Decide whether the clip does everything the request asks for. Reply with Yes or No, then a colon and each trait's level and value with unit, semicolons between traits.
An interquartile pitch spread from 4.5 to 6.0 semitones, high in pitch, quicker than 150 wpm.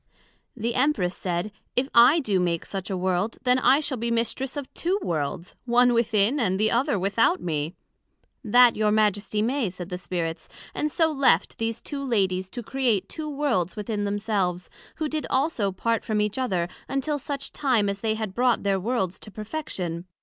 Yes: wide, 5.4 semitones; high, 220 Hz; average, 185 wpm